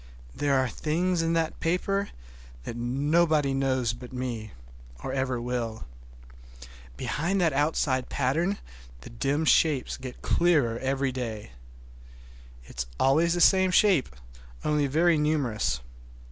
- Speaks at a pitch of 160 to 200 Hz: No, medium, 140 Hz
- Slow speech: Yes, slow, 125 wpm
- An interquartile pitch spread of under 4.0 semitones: No, average, 4.7 semitones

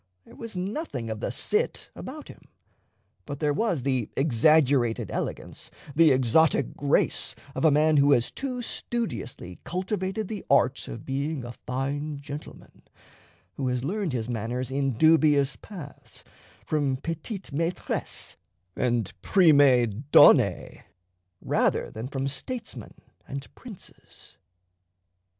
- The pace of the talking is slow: Yes, slow, 125 wpm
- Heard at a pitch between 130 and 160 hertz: Yes, medium, 140 Hz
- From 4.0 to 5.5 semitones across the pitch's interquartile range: Yes, average, 4.6 semitones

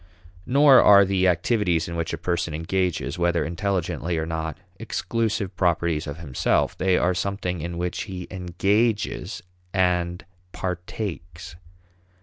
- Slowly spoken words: Yes, slow, 130 wpm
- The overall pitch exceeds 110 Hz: No, very low, 90 Hz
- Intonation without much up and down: Yes, narrow, 2.3 semitones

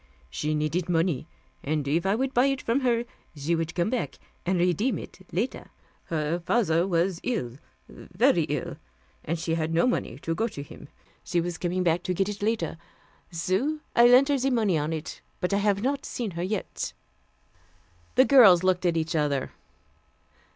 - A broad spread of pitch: Yes, wide, 5.7 semitones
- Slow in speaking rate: No, average, 185 wpm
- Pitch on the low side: No, medium, 180 Hz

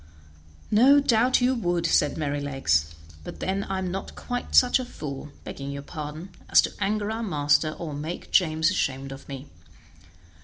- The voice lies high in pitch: No, medium, 160 Hz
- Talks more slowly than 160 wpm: No, average, 165 wpm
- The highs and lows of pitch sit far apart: Yes, wide, 6.6 semitones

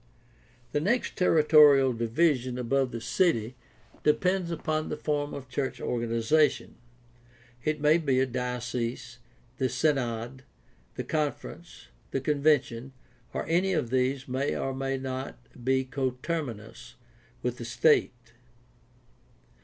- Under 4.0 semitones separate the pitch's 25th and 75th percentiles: Yes, average, 3.6 semitones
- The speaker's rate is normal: No, slow, 120 wpm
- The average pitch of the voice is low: Yes, low, 130 Hz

